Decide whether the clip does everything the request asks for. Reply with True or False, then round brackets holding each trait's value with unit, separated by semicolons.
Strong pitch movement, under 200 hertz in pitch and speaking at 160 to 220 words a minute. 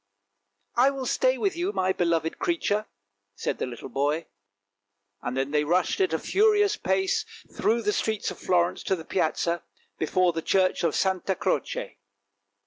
True (8.3 semitones; 185 Hz; 170 wpm)